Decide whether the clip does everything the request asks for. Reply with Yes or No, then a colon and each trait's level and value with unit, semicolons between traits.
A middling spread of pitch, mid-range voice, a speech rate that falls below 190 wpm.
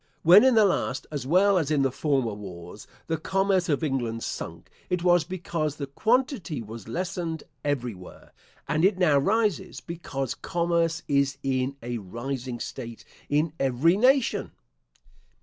No: wide, 5.7 semitones; medium, 150 Hz; average, 145 wpm